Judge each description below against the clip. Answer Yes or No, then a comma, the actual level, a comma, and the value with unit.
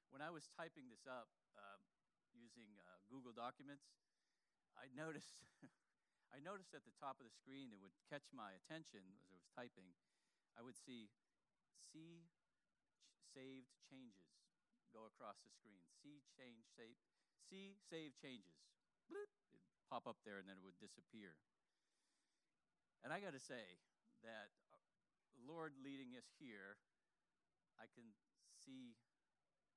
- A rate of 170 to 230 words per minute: No, average, 140 wpm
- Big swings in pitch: Yes, wide, 5.7 semitones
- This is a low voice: Yes, low, 130 Hz